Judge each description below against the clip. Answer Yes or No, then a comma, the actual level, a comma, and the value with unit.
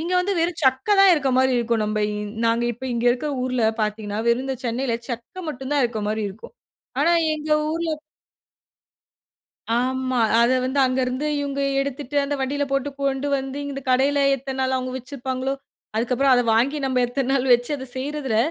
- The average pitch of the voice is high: Yes, very high, 260 Hz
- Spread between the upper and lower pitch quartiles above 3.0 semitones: No, narrow, 2.6 semitones